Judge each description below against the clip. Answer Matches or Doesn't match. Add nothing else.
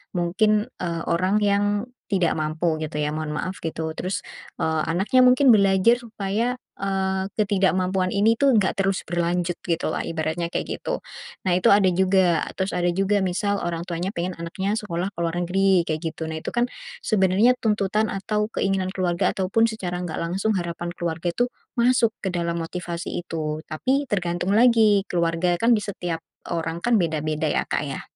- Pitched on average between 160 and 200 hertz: Matches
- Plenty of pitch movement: Doesn't match